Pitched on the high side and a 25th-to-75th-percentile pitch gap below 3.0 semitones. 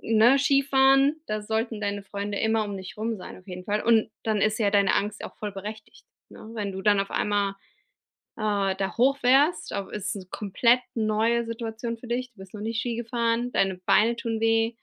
Yes: high, 220 Hz; narrow, 2.5 semitones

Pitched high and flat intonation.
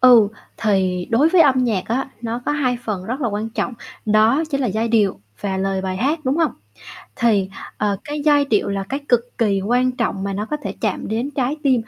No: high, 230 Hz; average, 4.8 semitones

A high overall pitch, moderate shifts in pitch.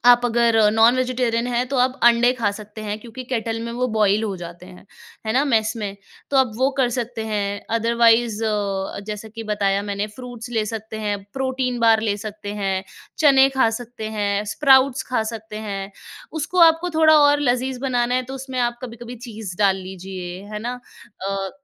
Yes: high, 225 Hz; average, 3.4 semitones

